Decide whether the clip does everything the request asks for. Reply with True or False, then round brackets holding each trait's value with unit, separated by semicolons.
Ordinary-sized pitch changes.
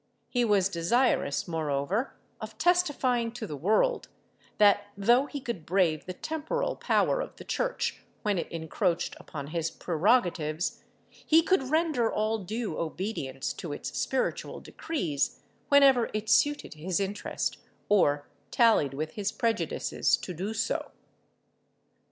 False (7.3 semitones)